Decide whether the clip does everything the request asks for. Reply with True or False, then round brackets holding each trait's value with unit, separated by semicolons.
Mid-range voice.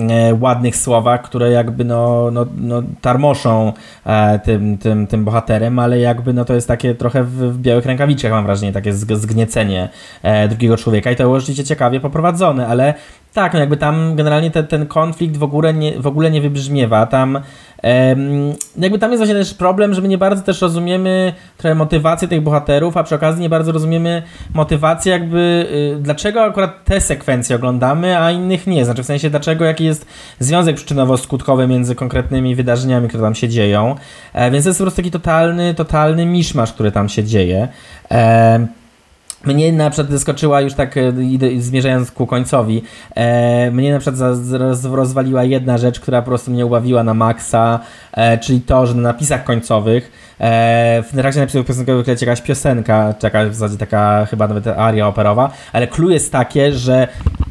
False (130 Hz)